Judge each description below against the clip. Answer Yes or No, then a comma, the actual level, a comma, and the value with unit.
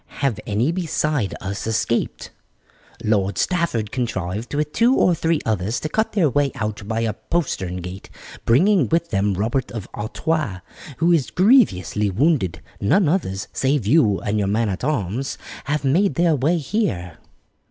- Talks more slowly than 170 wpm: Yes, average, 155 wpm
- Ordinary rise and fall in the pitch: No, wide, 8.0 semitones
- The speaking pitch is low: Yes, low, 120 Hz